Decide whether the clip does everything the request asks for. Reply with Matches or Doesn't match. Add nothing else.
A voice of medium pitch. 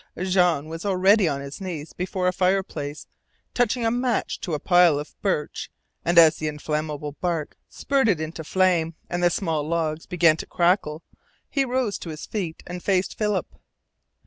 Matches